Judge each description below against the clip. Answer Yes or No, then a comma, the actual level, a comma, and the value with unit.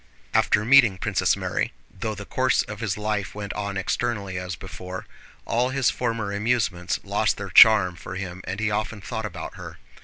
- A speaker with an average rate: Yes, average, 180 wpm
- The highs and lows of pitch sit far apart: No, average, 2.9 semitones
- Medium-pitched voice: No, low, 105 Hz